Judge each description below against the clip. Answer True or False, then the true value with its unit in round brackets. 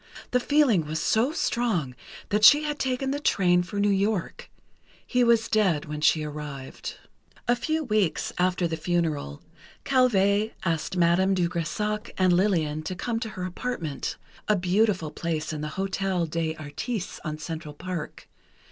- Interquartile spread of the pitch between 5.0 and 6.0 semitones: True (5.5 semitones)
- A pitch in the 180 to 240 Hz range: True (185 Hz)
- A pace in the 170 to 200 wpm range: False (155 wpm)